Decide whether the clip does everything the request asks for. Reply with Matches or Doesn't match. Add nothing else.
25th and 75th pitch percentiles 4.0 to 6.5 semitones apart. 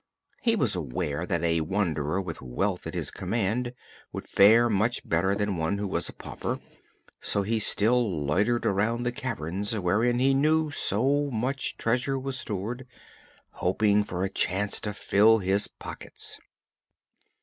Matches